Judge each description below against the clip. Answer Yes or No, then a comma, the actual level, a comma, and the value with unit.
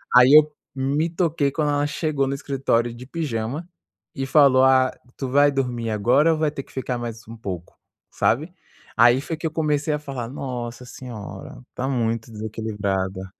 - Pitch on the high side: No, low, 130 Hz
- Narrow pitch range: No, average, 4.0 semitones